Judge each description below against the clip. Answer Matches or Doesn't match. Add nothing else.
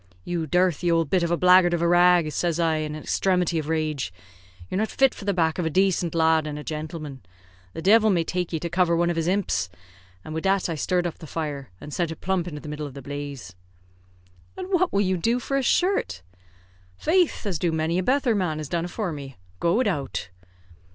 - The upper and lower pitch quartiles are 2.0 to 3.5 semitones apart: Matches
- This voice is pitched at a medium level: Matches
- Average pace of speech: Doesn't match